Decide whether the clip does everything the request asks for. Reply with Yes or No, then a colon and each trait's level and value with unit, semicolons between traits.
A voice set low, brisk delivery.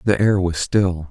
Yes: very low, 95 Hz; fast, 215 wpm